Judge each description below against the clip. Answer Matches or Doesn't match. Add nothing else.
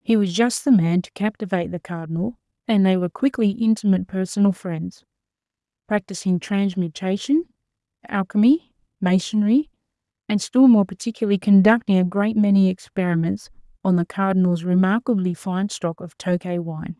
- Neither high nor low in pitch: Doesn't match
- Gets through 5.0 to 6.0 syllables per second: Matches